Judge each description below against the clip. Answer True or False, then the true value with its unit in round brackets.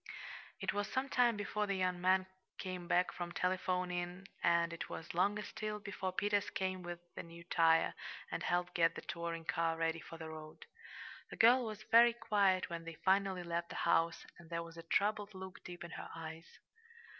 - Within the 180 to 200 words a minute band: True (190 wpm)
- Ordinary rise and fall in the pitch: True (3.1 semitones)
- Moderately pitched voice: True (180 Hz)